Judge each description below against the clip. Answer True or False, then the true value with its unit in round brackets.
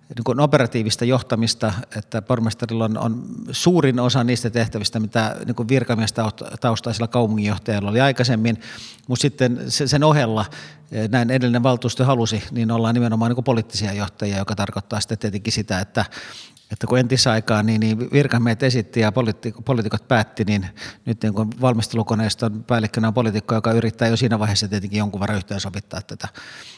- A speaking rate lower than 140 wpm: False (145 wpm)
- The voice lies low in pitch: True (115 Hz)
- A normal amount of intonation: False (2.2 semitones)